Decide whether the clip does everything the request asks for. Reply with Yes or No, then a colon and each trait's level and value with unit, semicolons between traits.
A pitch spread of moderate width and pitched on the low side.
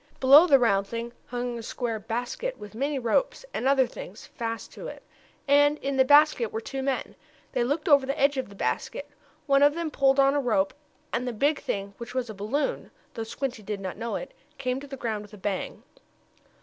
No: average, 3.9 semitones; very high, 255 Hz